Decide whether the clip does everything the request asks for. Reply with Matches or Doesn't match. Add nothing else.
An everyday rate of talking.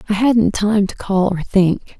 Doesn't match